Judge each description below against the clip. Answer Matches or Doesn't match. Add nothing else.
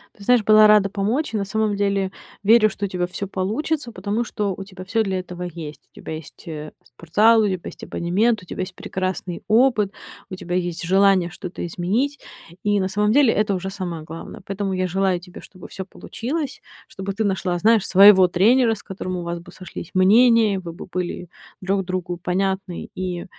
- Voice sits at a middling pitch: Doesn't match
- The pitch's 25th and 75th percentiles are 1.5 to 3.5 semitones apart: Matches